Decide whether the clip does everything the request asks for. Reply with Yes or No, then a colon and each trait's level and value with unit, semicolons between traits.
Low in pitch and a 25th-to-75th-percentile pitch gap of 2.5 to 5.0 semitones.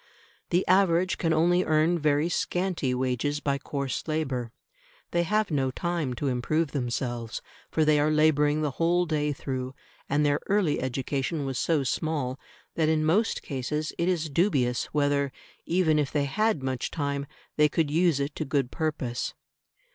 No: medium, 150 Hz; average, 3.4 semitones